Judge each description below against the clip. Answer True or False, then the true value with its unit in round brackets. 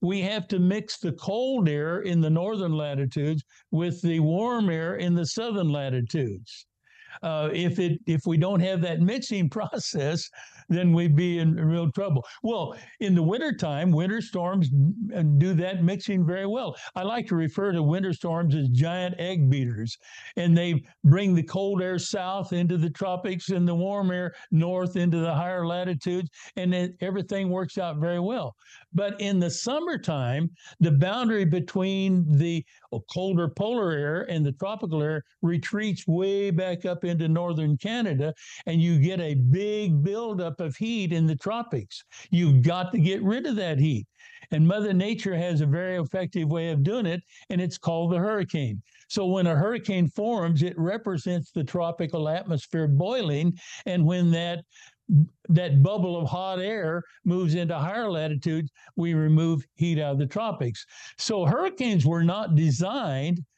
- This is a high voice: False (175 Hz)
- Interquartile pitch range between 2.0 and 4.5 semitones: True (3.0 semitones)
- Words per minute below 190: True (165 wpm)